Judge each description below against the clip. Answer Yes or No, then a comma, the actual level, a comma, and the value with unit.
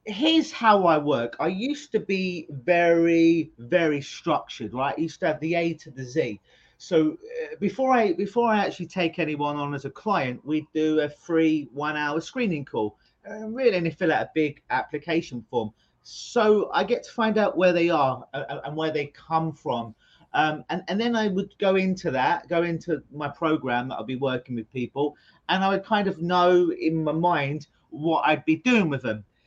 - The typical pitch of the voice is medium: Yes, medium, 165 Hz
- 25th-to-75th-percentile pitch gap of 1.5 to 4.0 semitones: No, average, 4.8 semitones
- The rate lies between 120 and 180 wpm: No, fast, 205 wpm